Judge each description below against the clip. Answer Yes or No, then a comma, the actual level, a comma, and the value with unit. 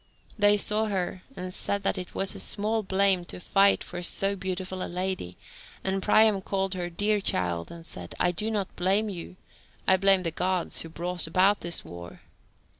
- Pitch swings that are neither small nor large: No, narrow, 2.1 semitones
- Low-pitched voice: No, high, 190 Hz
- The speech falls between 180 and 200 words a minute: Yes, average, 185 wpm